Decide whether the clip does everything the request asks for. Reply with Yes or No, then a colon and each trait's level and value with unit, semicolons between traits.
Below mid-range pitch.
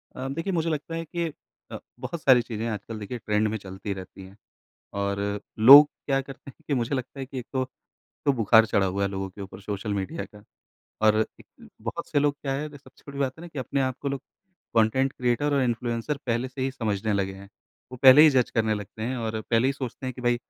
Yes: low, 125 Hz